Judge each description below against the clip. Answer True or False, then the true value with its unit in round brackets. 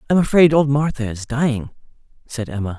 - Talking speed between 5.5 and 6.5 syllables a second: True (5.9 syllables/s)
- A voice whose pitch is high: False (130 Hz)